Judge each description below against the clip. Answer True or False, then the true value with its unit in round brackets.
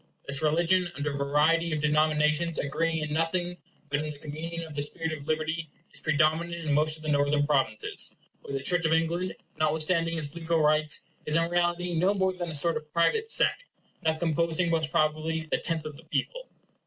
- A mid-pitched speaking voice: True (160 Hz)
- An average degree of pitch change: False (1.8 semitones)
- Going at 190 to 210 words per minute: True (200 wpm)